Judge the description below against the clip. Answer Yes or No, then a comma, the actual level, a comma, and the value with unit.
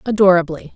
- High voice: No, medium, 180 Hz